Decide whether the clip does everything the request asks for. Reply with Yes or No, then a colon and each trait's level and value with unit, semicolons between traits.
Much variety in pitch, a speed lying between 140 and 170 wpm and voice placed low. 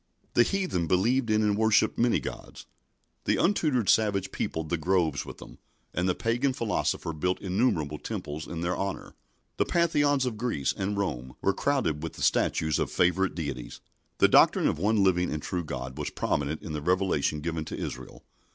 No: wide, 6.3 semitones; average, 180 wpm; very low, 90 Hz